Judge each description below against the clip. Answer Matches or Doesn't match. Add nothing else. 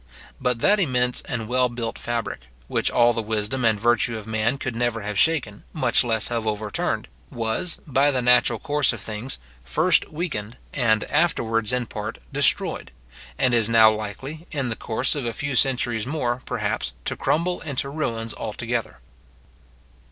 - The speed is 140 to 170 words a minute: Matches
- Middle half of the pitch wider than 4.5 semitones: Doesn't match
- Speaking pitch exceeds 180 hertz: Doesn't match